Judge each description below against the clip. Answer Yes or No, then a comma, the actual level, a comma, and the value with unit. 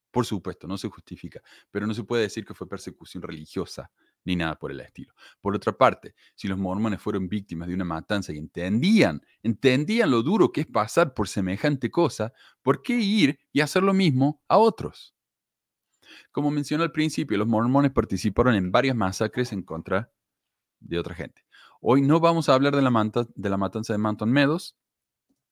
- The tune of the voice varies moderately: No, wide, 6.6 semitones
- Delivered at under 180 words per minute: No, average, 185 wpm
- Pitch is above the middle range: No, low, 110 Hz